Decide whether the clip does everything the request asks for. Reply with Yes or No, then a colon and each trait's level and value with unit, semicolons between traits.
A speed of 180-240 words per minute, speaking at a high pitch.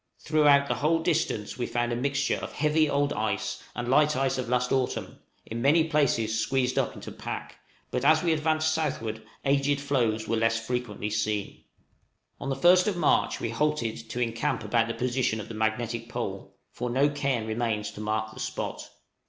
No: average, 190 wpm; low, 125 Hz